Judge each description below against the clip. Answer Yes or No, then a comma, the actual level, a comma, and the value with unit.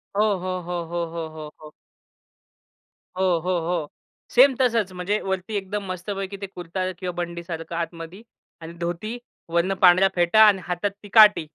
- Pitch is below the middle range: No, medium, 180 Hz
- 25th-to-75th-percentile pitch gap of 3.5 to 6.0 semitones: No, average, 2.8 semitones